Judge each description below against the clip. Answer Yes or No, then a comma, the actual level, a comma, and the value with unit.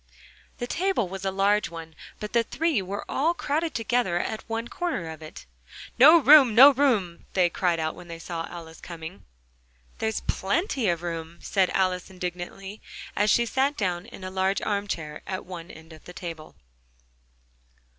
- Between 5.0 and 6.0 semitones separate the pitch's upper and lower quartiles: Yes, wide, 5.6 semitones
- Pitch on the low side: No, high, 190 Hz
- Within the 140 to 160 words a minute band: No, average, 175 wpm